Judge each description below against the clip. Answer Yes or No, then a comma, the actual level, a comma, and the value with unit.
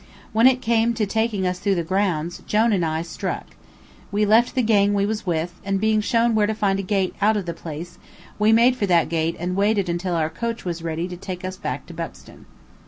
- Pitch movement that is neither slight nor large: Yes, average, 3.8 semitones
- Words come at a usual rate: No, fast, 235 wpm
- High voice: Yes, high, 195 Hz